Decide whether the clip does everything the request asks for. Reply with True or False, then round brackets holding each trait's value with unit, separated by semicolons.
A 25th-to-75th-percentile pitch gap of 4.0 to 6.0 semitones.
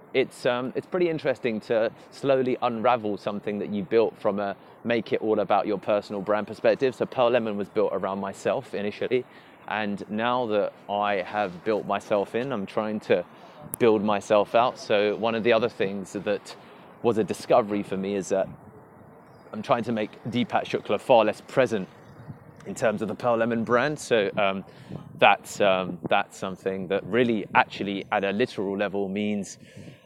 False (2.5 semitones)